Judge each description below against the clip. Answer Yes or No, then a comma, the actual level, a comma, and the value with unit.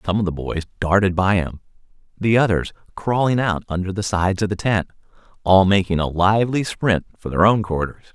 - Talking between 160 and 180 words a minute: No, average, 190 wpm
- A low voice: Yes, very low, 95 Hz